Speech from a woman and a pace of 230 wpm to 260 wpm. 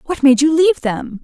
Yes: female; fast, 245 wpm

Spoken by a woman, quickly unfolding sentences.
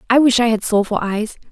Yes: female; fast, 240 wpm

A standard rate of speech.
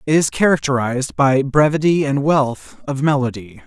Yes: average, 145 wpm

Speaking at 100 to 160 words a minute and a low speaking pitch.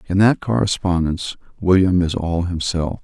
Yes: average, 140 wpm; very low, 90 Hz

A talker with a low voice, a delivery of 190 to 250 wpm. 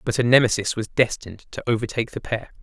Yes: low, 115 Hz; fast, 205 wpm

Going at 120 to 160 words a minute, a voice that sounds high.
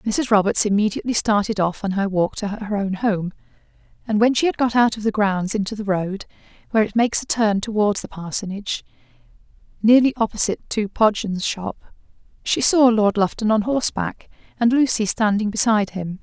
No: average, 175 wpm; high, 210 Hz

